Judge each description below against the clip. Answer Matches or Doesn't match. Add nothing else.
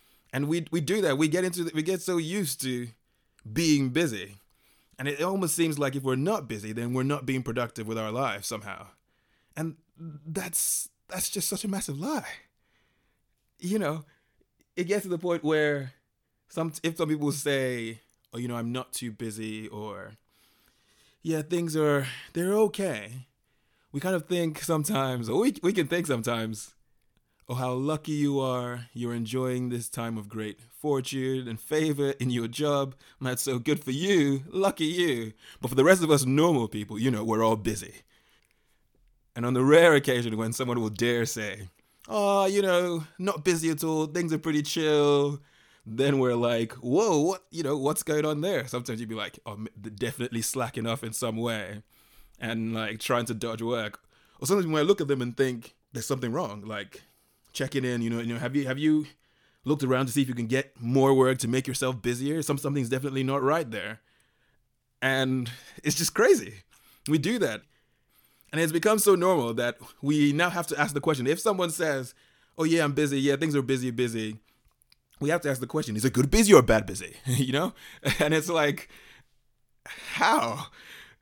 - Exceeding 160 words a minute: Matches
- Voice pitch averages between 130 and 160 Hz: Matches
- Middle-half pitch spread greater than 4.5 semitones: Matches